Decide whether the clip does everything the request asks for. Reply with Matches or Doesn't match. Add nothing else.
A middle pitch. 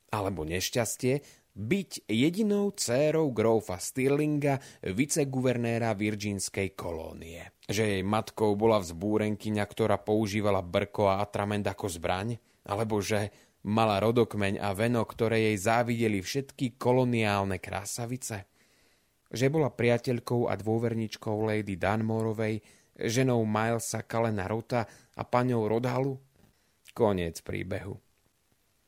Doesn't match